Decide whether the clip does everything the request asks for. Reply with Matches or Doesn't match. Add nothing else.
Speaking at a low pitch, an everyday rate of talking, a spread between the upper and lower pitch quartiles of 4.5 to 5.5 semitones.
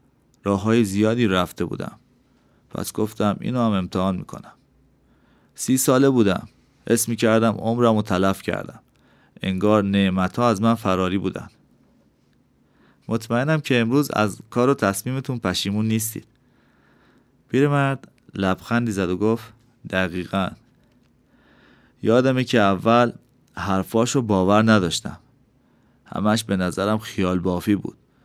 Doesn't match